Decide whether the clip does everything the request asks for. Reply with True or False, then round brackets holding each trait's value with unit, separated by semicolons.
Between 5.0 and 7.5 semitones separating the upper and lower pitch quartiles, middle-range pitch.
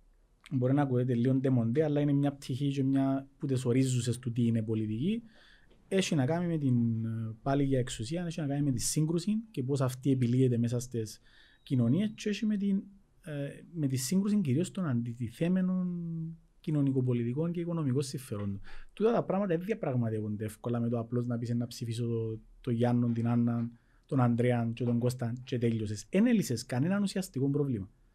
False (5.4 semitones; 130 Hz)